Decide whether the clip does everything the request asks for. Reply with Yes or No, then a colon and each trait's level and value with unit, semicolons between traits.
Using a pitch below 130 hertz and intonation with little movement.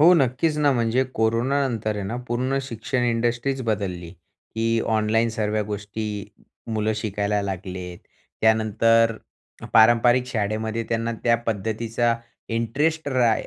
Yes: low, 115 Hz; narrow, 2.1 semitones